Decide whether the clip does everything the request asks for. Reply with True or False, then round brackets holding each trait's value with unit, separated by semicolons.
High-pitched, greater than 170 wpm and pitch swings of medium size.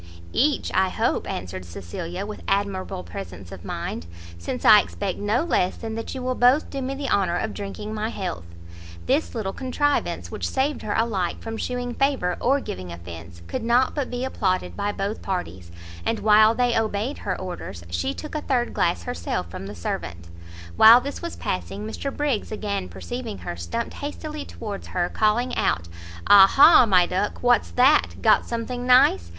False (210 Hz; 180 wpm; 6.2 semitones)